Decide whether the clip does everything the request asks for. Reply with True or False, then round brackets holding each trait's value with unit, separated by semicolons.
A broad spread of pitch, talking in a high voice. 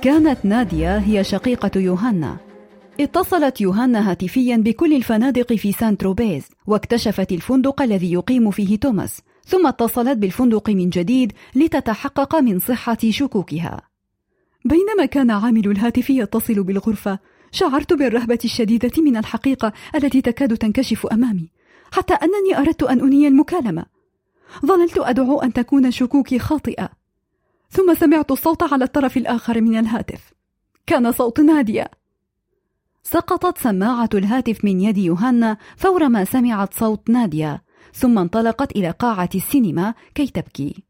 False (5.0 semitones; 240 Hz)